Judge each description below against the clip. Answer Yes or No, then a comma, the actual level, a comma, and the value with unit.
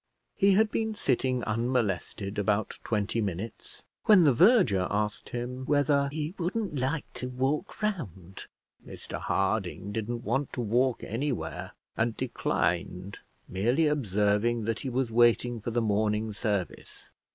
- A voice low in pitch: Yes, low, 120 Hz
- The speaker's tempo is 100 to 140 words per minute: Yes, slow, 135 wpm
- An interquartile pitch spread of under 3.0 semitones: No, average, 5.2 semitones